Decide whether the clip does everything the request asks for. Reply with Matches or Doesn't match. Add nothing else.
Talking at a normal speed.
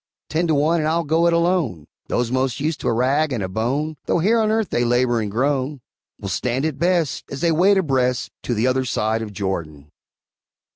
Doesn't match